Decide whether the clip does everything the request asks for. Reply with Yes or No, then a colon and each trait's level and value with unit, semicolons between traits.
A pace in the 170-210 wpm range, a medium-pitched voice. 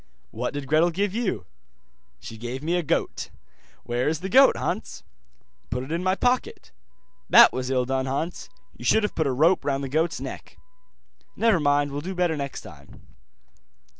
Yes: average, 180 wpm; medium, 150 Hz